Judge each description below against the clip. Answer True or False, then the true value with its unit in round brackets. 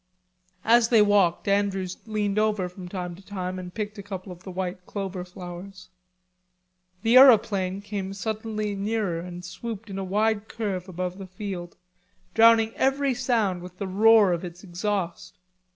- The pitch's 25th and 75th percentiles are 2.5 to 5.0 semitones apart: True (2.9 semitones)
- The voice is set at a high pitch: True (195 Hz)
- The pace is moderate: True (160 wpm)